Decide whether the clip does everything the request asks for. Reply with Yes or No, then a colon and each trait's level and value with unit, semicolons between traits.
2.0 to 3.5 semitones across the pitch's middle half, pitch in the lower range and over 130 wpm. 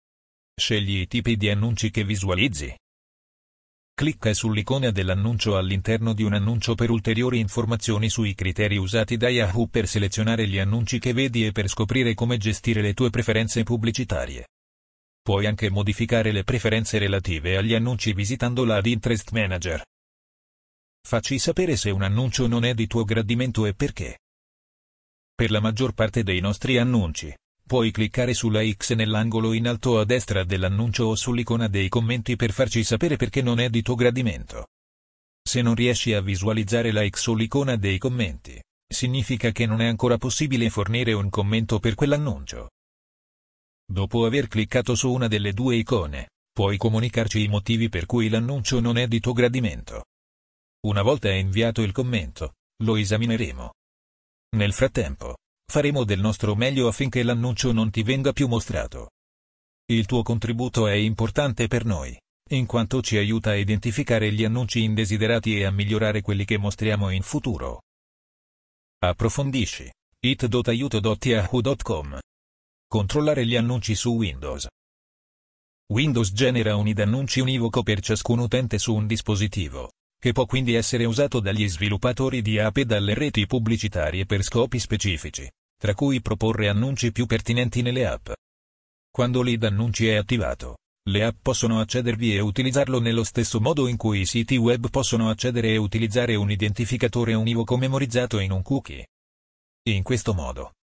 Yes: average, 3.0 semitones; low, 110 Hz; average, 150 wpm